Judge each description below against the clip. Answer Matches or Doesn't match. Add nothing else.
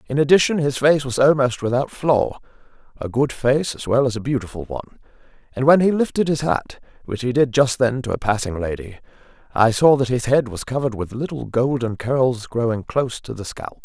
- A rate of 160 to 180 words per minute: Doesn't match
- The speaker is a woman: Doesn't match